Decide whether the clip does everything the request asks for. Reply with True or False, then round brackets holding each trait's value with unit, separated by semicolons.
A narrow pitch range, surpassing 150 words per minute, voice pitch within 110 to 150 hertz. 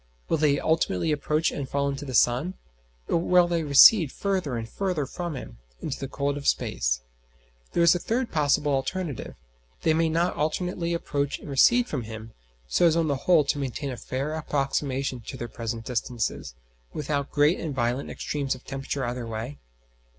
False (4.1 semitones; 180 wpm; 140 Hz)